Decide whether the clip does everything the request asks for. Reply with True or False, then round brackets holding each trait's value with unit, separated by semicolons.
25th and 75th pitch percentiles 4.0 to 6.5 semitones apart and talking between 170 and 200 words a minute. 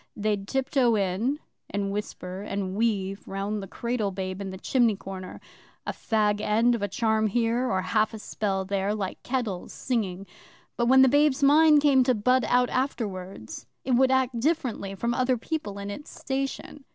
True (4.5 semitones; 175 wpm)